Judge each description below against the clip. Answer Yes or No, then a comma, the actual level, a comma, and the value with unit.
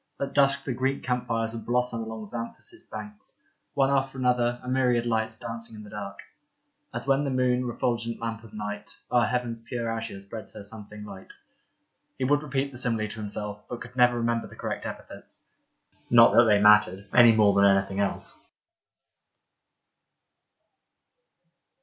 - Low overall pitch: Yes, low, 115 Hz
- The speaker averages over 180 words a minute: No, average, 170 wpm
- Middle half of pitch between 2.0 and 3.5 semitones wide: Yes, average, 2.8 semitones